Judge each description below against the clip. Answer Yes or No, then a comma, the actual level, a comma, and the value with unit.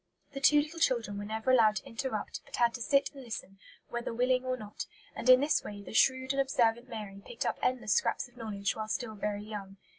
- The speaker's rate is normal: No, fast, 230 wpm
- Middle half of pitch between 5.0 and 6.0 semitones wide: No, average, 3.5 semitones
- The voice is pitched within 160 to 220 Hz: No, high, 235 Hz